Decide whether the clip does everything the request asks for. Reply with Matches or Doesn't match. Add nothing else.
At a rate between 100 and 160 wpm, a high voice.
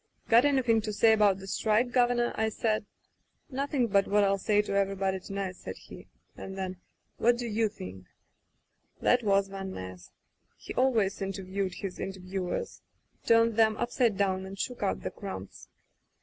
Doesn't match